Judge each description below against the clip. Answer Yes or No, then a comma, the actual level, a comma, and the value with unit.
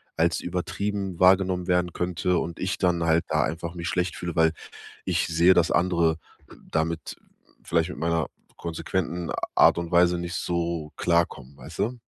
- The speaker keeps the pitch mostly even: Yes, narrow, 1.4 semitones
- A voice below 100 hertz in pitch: Yes, very low, 85 Hz